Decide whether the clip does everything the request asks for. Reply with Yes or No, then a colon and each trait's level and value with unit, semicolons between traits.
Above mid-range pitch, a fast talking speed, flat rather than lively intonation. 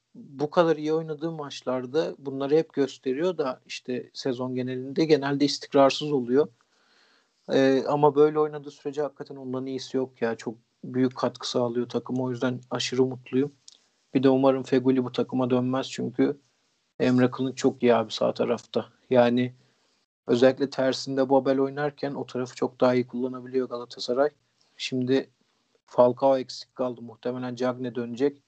No: low, 130 Hz; fast, 145 wpm; narrow, 1.9 semitones